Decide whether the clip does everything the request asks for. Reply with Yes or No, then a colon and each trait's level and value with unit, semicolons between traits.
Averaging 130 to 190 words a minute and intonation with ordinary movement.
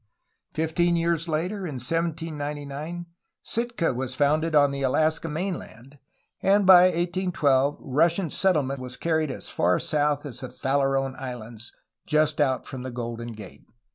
Yes: average, 140 wpm; average, 4.1 semitones